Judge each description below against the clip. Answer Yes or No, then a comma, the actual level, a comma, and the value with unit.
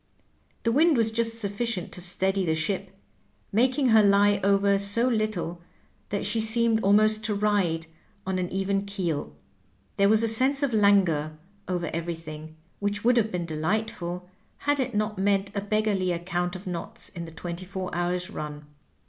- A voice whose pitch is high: Yes, high, 200 Hz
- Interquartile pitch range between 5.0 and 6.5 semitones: No, average, 3.6 semitones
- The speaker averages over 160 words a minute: Yes, average, 170 wpm